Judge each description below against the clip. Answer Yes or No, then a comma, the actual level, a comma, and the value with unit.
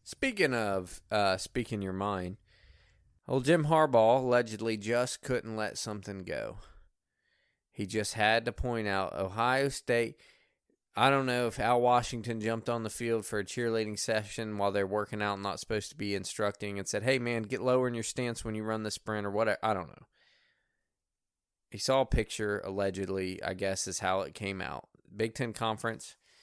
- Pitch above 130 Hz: No, low, 110 Hz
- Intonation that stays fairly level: No, average, 3.2 semitones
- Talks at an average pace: Yes, average, 185 wpm